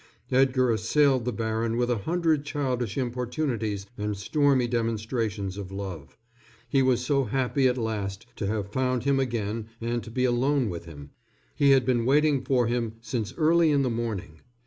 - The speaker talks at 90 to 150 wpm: No, average, 170 wpm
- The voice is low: Yes, low, 120 Hz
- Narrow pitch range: No, average, 3.4 semitones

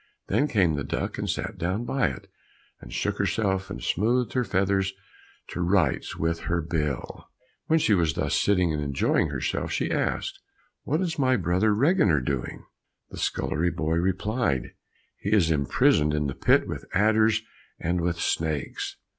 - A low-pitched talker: Yes, very low, 90 Hz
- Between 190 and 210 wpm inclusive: No, average, 165 wpm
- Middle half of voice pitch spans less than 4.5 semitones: No, wide, 5.6 semitones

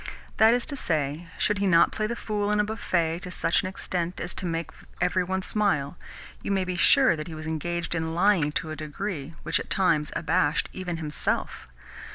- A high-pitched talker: No, medium, 175 Hz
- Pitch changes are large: No, average, 3.7 semitones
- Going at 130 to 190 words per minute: No, fast, 205 wpm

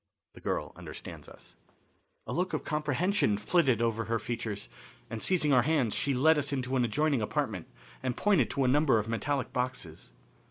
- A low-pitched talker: Yes, low, 130 Hz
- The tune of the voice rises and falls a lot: No, average, 4.7 semitones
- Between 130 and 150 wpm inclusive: No, average, 175 wpm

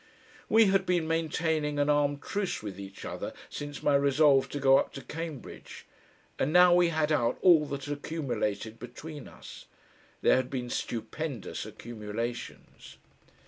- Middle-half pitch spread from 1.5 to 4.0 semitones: No, average, 4.5 semitones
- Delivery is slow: No, average, 150 wpm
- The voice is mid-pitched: Yes, medium, 145 Hz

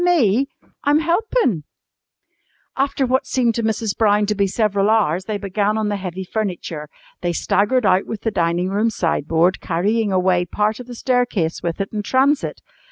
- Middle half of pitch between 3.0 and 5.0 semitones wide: Yes, average, 4.3 semitones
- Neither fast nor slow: Yes, average, 170 wpm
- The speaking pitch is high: Yes, high, 210 Hz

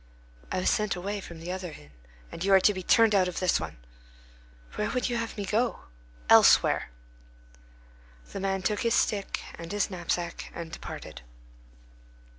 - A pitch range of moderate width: Yes, average, 3.1 semitones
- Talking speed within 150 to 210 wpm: Yes, average, 170 wpm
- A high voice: Yes, high, 195 Hz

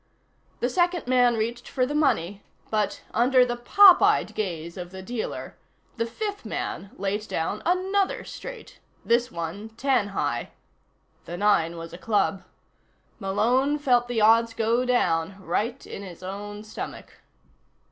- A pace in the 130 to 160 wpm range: Yes, average, 140 wpm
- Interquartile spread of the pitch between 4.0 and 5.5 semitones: Yes, average, 4.5 semitones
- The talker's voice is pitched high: Yes, high, 225 Hz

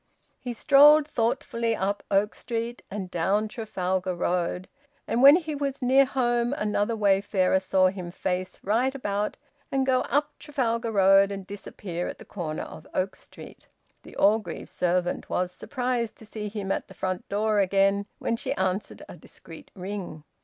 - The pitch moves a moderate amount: Yes, average, 4.2 semitones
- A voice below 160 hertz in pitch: No, high, 205 Hz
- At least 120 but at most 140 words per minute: No, average, 160 wpm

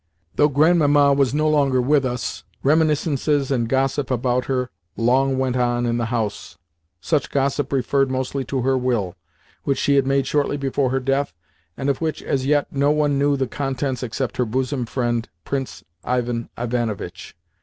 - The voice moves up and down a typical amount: No, narrow, 2.3 semitones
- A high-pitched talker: No, low, 135 Hz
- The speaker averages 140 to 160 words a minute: No, average, 170 wpm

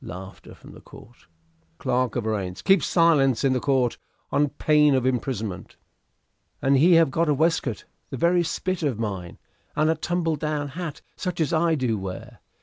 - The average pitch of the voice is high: No, medium, 140 Hz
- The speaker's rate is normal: Yes, average, 160 wpm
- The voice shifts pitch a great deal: Yes, wide, 5.8 semitones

